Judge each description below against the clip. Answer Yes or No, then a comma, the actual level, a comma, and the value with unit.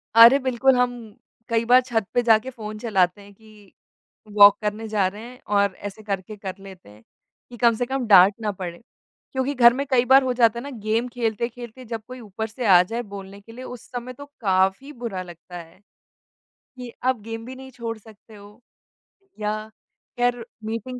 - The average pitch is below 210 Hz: No, high, 225 Hz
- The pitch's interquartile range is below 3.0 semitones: No, average, 3.3 semitones